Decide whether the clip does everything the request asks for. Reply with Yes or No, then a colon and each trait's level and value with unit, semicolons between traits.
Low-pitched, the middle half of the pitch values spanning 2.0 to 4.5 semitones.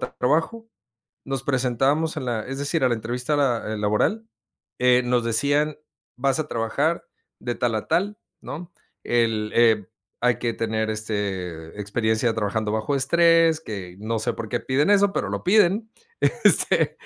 No: low, 125 Hz; wide, 5.4 semitones